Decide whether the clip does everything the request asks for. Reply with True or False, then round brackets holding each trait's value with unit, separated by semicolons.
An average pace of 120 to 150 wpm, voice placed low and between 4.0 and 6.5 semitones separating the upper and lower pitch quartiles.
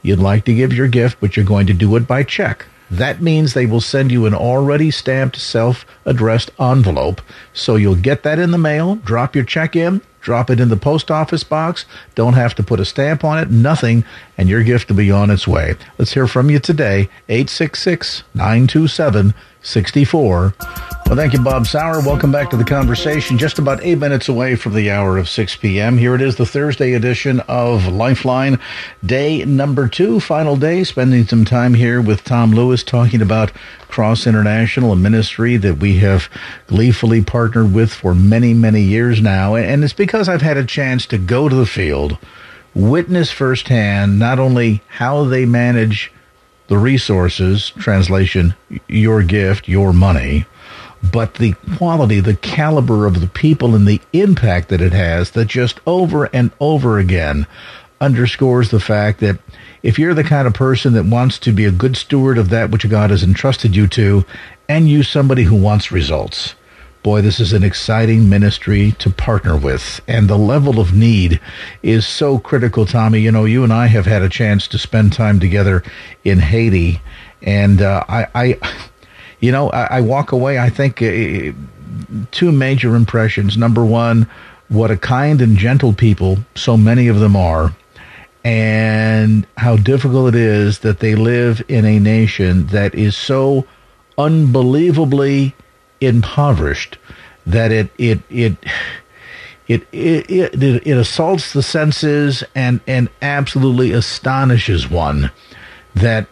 False (165 wpm; 115 Hz; 4.3 semitones)